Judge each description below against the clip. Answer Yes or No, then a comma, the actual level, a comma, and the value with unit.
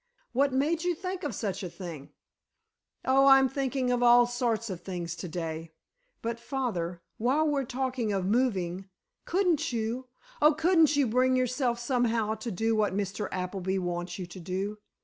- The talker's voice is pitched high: Yes, high, 235 Hz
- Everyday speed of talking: Yes, average, 160 wpm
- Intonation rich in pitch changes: Yes, wide, 5.9 semitones